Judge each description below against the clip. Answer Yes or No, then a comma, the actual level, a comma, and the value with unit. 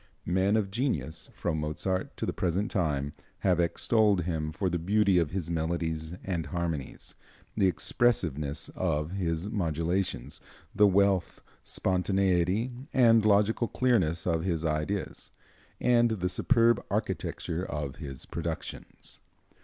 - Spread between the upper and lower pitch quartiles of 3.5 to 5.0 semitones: Yes, average, 3.9 semitones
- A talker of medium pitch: No, very low, 90 Hz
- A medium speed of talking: No, slow, 125 wpm